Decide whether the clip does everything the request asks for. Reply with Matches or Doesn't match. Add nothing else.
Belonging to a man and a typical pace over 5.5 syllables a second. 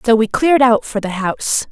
Doesn't match